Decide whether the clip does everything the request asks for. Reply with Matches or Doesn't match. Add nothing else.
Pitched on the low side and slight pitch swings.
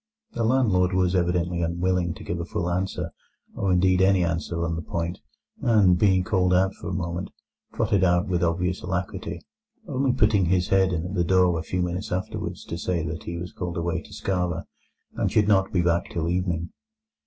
Matches